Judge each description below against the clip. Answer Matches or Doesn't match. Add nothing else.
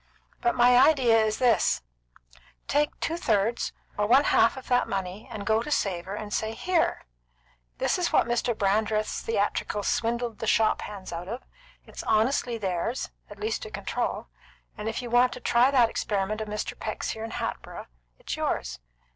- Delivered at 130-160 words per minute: Doesn't match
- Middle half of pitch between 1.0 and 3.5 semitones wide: Matches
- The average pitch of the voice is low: Doesn't match